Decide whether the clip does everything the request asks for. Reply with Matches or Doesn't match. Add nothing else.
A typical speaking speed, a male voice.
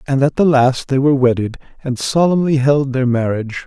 Matches